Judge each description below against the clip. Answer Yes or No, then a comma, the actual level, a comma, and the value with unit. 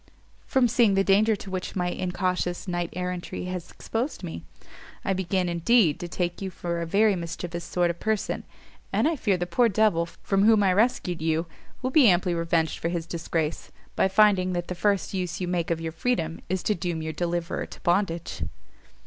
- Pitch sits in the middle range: Yes, medium, 180 Hz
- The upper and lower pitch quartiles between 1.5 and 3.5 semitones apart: Yes, average, 2.8 semitones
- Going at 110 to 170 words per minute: No, average, 195 wpm